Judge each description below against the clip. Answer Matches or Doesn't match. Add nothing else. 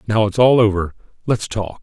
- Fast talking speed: Doesn't match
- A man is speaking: Matches